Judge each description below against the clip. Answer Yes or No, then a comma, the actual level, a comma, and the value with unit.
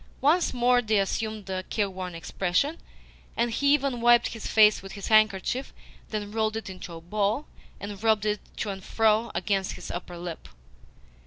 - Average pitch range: Yes, average, 3.3 semitones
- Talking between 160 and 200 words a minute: Yes, average, 170 wpm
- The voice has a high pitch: Yes, high, 215 Hz